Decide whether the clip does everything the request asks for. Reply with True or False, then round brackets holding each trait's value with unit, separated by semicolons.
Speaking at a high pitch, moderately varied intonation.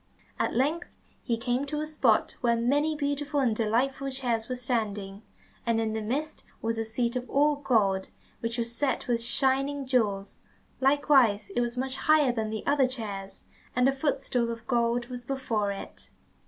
True (245 Hz; 3.3 semitones)